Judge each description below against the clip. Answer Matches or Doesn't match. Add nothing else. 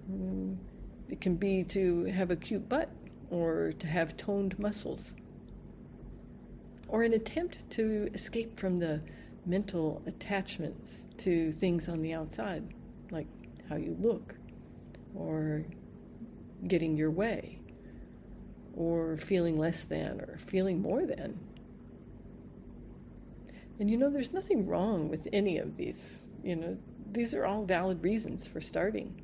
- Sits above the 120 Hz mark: Matches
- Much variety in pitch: Doesn't match